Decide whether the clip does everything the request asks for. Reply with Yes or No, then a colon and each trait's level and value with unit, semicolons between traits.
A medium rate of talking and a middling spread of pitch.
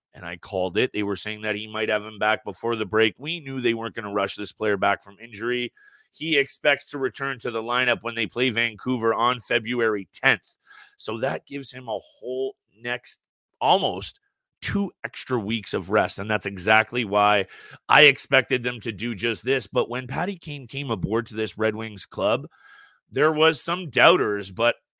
Yes: average, 195 wpm; average, 3.8 semitones